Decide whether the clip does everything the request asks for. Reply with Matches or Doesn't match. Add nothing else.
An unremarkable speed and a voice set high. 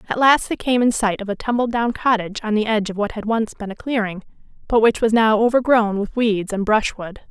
Doesn't match